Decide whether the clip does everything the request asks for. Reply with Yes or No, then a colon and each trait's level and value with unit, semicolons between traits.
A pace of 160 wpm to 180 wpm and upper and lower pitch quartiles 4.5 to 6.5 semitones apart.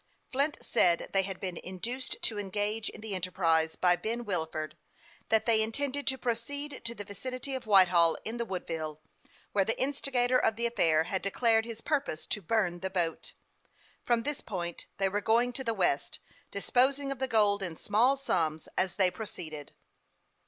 Yes: average, 175 wpm; average, 5.2 semitones